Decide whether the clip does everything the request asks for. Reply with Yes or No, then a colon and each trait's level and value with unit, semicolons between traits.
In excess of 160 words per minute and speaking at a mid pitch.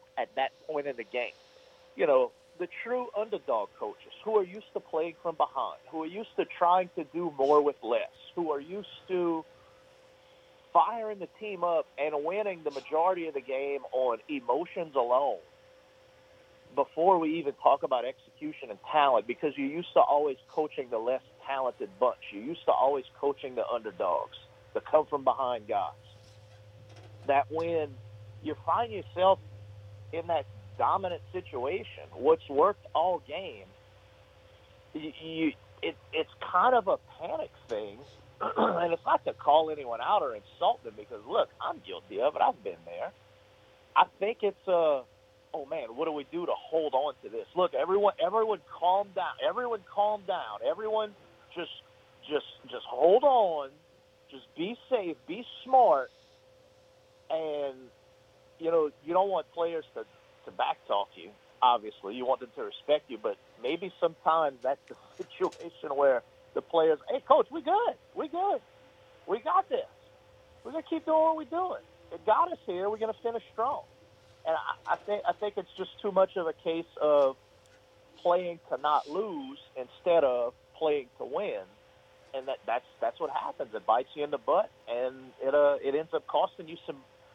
Yes: average, 170 wpm; medium, 180 Hz